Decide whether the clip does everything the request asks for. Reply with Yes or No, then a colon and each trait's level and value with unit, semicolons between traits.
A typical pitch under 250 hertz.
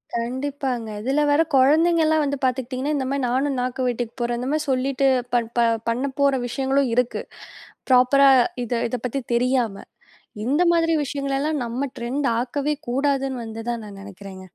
No: very high, 260 Hz